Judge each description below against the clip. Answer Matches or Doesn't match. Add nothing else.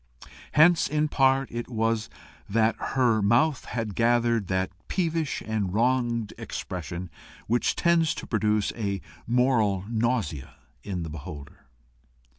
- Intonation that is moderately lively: Matches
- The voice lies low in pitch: Matches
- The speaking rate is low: Matches